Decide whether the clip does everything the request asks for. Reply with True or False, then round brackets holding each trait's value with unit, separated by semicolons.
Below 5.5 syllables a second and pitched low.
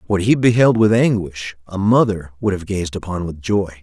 True (4.9 syllables/s; 100 Hz)